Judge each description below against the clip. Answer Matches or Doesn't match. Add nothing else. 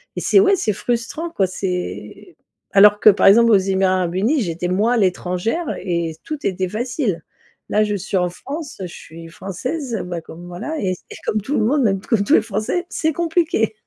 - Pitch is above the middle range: Matches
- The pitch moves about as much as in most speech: Doesn't match